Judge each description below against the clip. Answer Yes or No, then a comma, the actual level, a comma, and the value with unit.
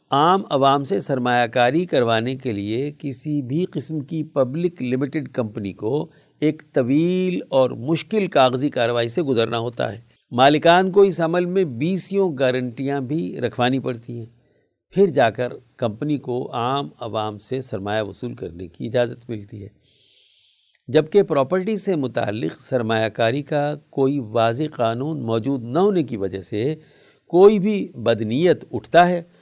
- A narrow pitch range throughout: No, average, 4.8 semitones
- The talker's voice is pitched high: No, low, 135 Hz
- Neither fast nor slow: Yes, average, 150 wpm